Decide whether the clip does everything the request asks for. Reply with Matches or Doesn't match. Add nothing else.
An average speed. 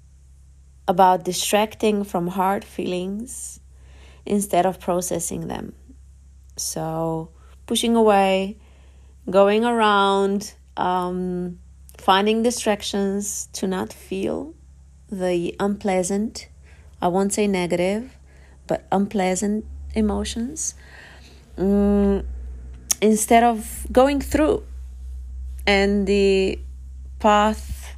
Doesn't match